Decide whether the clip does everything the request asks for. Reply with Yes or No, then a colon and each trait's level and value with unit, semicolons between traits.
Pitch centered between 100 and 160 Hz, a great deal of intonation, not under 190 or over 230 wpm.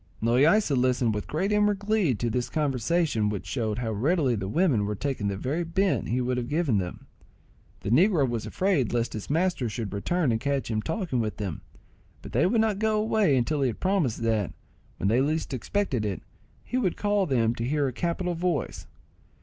Yes: low, 135 Hz; wide, 7.6 semitones; average, 200 wpm